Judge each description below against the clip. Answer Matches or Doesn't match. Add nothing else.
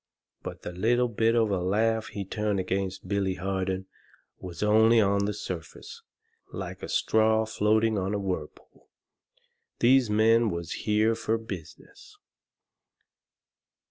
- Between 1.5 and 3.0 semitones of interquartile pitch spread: Matches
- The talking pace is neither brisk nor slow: Doesn't match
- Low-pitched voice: Matches